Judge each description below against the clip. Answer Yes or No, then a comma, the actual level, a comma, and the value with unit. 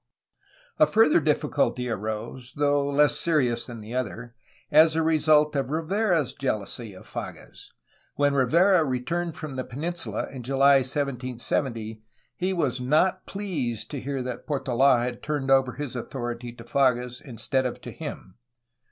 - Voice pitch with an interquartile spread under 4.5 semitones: Yes, average, 3.8 semitones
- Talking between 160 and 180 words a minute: No, average, 150 wpm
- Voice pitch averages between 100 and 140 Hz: Yes, low, 135 Hz